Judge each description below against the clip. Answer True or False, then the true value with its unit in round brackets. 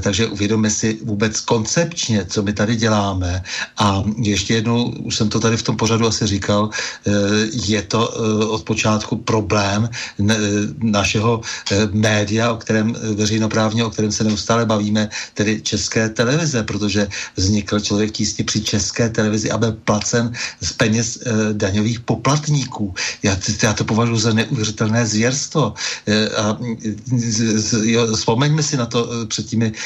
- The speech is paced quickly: False (135 wpm)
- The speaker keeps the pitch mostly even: True (1.7 semitones)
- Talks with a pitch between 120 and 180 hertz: False (110 Hz)